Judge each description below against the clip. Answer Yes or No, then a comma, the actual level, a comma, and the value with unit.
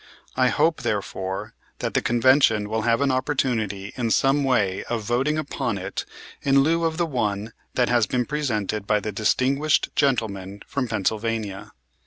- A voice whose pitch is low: Yes, low, 115 Hz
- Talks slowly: No, average, 160 wpm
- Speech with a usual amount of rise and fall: Yes, average, 4.5 semitones